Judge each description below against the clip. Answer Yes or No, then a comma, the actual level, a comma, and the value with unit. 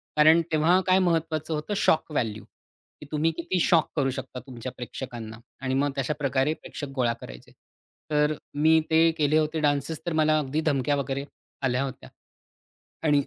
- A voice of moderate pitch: Yes, medium, 150 Hz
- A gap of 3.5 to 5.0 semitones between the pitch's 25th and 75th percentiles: No, average, 3.0 semitones